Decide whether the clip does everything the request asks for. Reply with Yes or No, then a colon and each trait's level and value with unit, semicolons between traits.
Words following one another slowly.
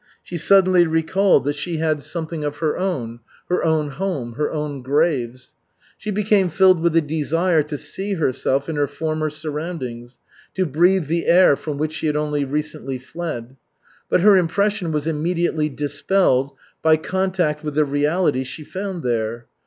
No: average, 165 wpm